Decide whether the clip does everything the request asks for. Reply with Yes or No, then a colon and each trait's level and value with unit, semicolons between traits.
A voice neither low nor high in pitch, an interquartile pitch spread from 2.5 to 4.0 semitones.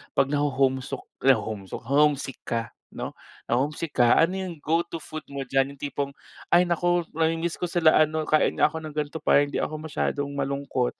Yes: medium, 145 Hz; average, 2.9 semitones